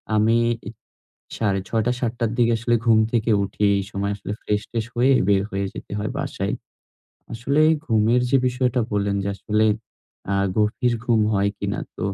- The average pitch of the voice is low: Yes, low, 110 Hz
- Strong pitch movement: No, narrow, 2.6 semitones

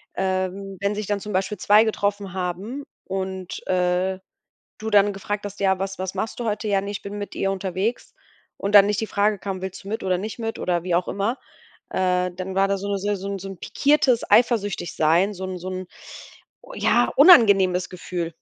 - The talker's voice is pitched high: Yes, high, 195 Hz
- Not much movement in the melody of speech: Yes, narrow, 1.8 semitones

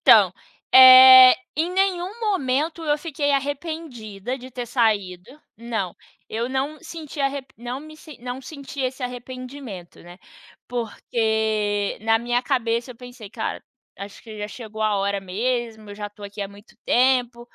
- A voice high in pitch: Yes, high, 245 Hz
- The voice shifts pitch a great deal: No, average, 3.8 semitones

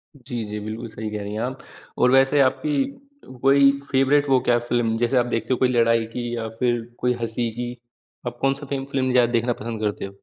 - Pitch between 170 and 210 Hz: No, low, 120 Hz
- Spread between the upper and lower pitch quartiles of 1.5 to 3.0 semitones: Yes, narrow, 2.6 semitones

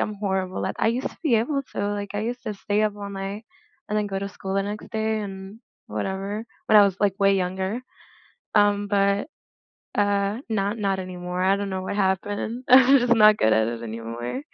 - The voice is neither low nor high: No, high, 200 Hz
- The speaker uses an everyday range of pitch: No, narrow, 1.8 semitones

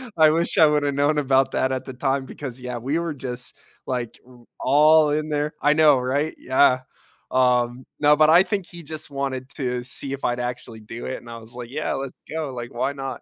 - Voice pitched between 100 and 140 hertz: Yes, low, 135 Hz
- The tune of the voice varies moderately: Yes, average, 3.1 semitones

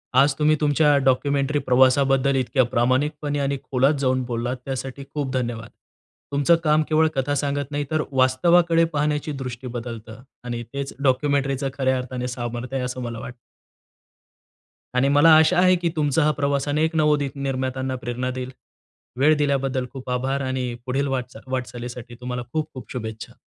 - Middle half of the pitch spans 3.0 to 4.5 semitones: No, narrow, 2.4 semitones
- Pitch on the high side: No, low, 135 Hz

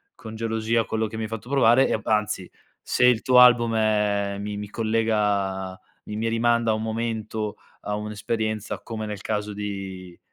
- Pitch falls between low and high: No, low, 110 Hz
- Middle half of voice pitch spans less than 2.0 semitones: Yes, narrow, 1.6 semitones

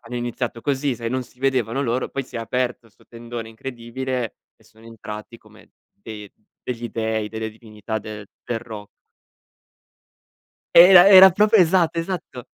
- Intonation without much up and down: No, average, 3.2 semitones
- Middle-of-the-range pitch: No, low, 120 Hz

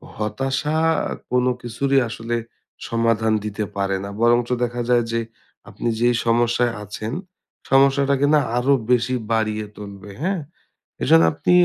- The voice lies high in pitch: No, low, 120 Hz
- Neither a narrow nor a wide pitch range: Yes, average, 3.2 semitones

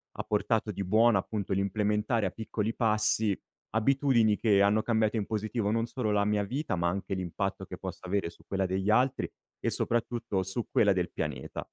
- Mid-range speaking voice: No, low, 105 Hz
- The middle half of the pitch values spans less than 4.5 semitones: Yes, narrow, 2.4 semitones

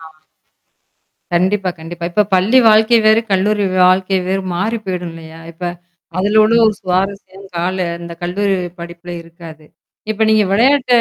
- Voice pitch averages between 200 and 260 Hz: No, high, 190 Hz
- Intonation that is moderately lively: Yes, average, 3.5 semitones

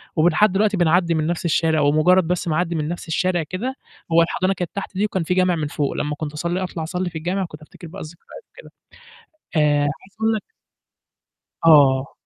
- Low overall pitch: No, medium, 170 Hz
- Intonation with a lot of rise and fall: No, average, 2.9 semitones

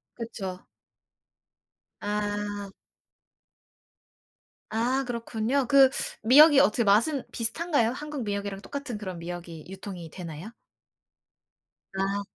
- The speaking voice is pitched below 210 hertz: No, high, 215 Hz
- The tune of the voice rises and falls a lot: No, average, 4.5 semitones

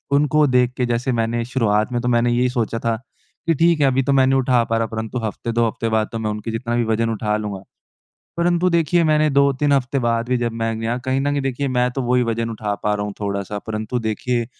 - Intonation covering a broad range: No, average, 2.8 semitones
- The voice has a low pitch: Yes, low, 120 Hz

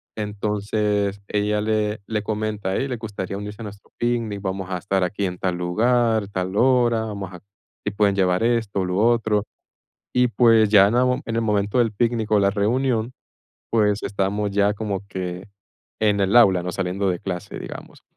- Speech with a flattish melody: Yes, narrow, 2.3 semitones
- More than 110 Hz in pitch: No, low, 105 Hz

